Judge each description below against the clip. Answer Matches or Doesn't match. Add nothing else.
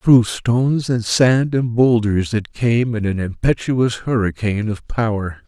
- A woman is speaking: Doesn't match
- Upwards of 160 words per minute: Doesn't match